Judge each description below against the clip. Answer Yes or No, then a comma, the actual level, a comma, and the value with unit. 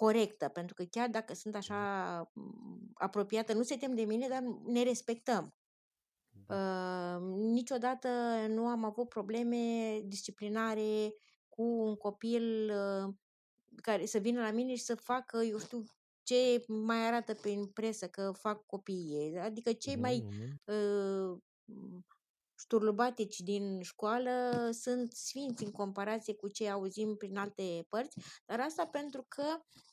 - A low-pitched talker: No, high, 220 Hz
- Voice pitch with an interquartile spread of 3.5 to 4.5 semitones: No, average, 2.8 semitones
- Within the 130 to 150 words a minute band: Yes, average, 135 wpm